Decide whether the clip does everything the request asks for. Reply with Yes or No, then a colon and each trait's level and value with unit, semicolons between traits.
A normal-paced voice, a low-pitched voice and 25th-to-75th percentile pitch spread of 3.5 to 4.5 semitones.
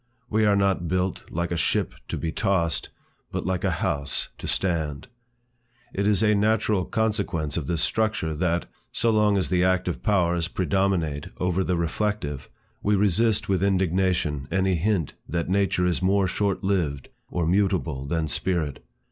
No: average, 160 wpm; very low, 90 Hz; average, 3.1 semitones